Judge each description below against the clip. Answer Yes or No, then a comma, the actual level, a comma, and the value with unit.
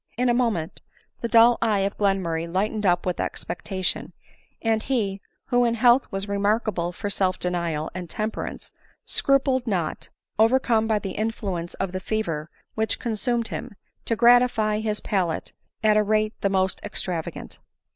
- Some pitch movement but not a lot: Yes, average, 3.5 semitones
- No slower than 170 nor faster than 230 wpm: No, average, 155 wpm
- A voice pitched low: No, high, 210 Hz